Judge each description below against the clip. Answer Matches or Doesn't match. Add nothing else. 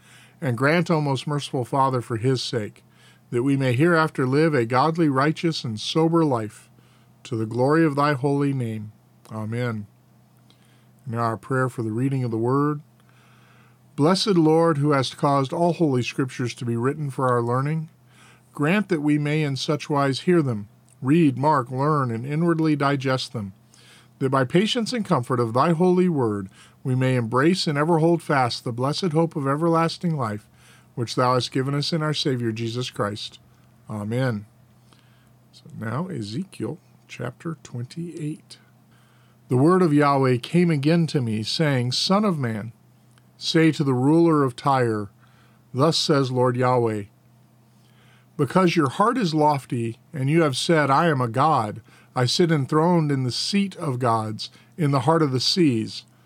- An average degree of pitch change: Matches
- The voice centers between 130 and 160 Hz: Matches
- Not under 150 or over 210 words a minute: Matches